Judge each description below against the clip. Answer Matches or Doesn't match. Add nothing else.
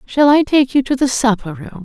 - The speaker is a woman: Matches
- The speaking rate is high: Matches